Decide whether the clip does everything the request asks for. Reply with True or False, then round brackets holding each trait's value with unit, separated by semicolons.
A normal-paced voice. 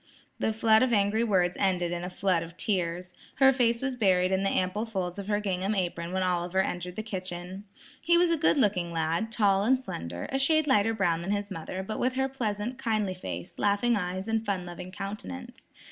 False (210 wpm)